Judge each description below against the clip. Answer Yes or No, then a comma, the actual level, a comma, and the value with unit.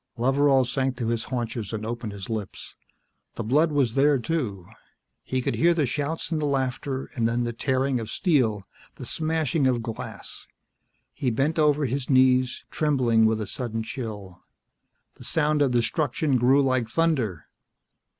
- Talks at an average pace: Yes, average, 160 wpm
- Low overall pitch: Yes, low, 130 Hz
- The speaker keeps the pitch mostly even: No, average, 4.0 semitones